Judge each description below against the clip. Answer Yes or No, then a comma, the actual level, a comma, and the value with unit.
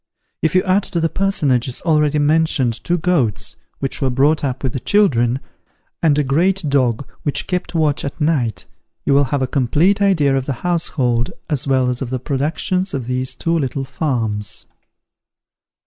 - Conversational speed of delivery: Yes, average, 175 wpm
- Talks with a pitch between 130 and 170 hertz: Yes, medium, 140 Hz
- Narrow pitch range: No, average, 4.3 semitones